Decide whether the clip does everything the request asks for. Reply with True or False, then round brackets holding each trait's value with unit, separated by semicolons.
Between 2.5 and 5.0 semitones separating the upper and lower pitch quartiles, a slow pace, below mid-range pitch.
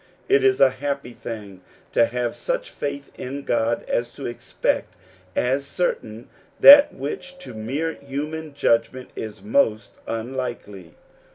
True (3.8 semitones; 130 wpm; 130 Hz)